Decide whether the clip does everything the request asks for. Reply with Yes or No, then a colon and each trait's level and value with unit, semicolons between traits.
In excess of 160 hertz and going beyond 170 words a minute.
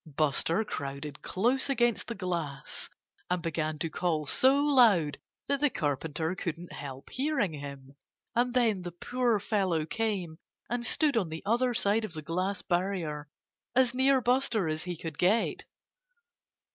No: medium, 185 Hz; average, 150 wpm